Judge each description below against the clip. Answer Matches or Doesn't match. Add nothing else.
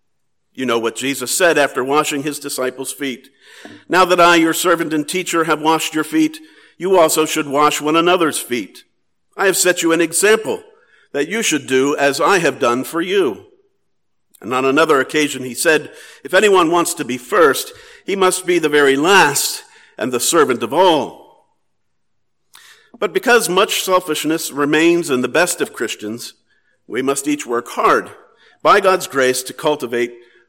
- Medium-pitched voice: Matches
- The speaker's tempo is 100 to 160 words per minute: Doesn't match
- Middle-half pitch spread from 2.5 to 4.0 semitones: Doesn't match